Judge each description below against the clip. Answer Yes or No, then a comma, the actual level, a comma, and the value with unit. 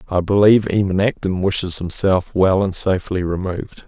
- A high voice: No, very low, 95 Hz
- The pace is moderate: Yes, average, 155 wpm